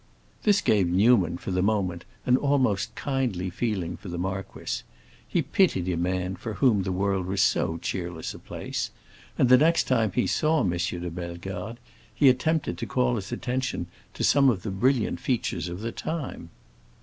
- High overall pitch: No, low, 100 Hz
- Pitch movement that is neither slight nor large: No, wide, 6.3 semitones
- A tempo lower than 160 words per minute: No, average, 175 wpm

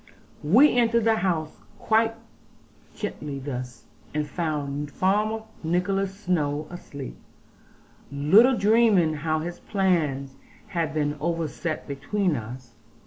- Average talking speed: No, slow, 105 wpm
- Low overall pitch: No, medium, 165 Hz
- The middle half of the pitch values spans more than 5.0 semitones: Yes, wide, 5.5 semitones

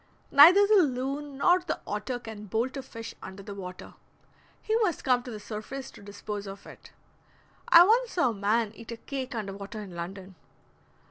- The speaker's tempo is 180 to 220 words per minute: Yes, average, 190 wpm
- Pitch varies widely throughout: Yes, wide, 5.7 semitones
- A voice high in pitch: Yes, high, 230 Hz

